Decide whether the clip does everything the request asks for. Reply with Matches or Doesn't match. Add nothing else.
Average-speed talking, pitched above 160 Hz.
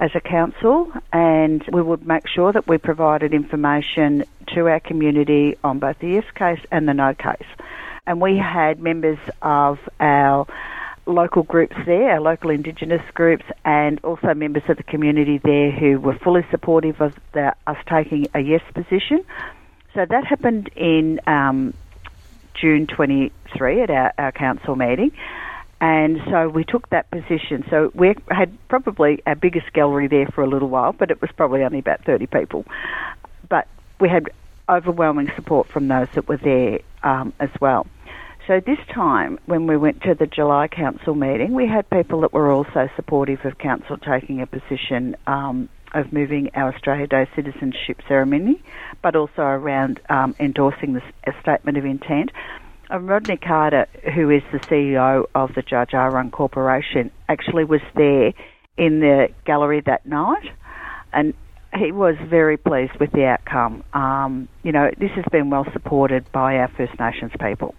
Doesn't match